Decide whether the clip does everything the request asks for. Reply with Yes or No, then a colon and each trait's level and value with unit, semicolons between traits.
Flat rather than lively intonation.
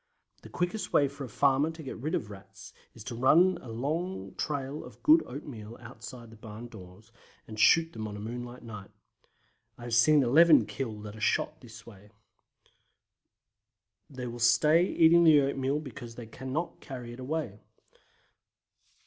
No: average, 5.0 semitones